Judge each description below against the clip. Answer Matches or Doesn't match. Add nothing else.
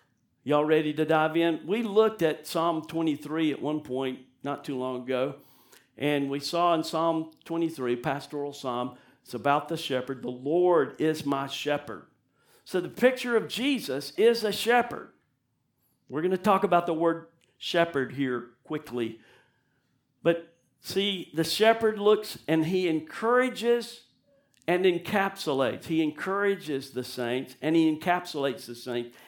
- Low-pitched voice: Doesn't match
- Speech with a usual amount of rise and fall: Matches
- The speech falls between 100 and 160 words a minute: Matches